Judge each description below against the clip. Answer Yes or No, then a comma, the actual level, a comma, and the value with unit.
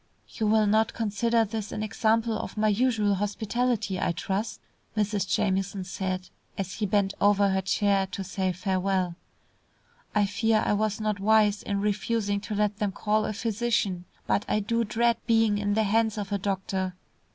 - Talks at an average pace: Yes, average, 175 wpm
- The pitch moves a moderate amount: No, narrow, 2.0 semitones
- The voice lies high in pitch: Yes, high, 205 Hz